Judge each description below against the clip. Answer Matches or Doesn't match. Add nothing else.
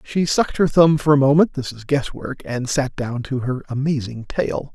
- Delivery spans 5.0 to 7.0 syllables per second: Doesn't match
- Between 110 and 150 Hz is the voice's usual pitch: Matches